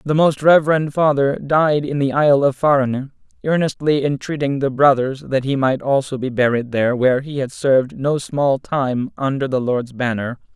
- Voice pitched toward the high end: No, low, 135 Hz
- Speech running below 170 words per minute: No, average, 180 wpm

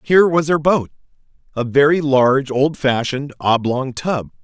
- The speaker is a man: Yes, male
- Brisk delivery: No, slow, 135 wpm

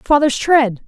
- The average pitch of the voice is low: No, very high, 270 Hz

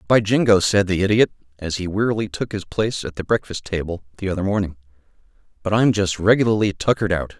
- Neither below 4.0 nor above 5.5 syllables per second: No, 6.4 syllables/s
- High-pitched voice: No, low, 100 Hz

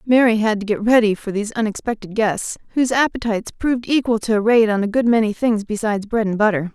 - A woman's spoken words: Yes, female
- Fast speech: Yes, fast, 220 wpm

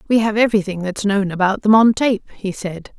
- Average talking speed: No, fast, 220 wpm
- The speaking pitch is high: Yes, high, 205 Hz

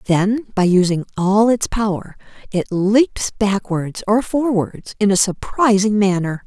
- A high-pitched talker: Yes, high, 205 Hz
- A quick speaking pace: No, average, 140 wpm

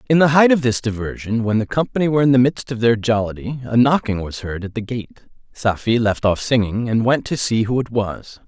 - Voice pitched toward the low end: Yes, low, 120 Hz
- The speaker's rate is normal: No, fast, 240 wpm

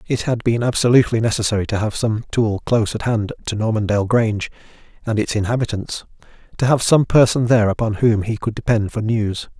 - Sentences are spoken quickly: No, average, 190 wpm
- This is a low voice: Yes, low, 110 Hz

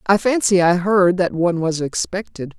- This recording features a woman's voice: Yes, female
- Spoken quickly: No, average, 185 wpm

